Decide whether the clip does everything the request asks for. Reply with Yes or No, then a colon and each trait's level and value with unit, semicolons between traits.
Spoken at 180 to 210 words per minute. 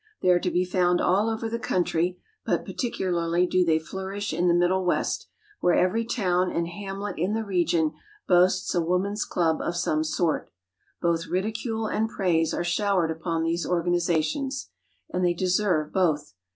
No: average, 165 wpm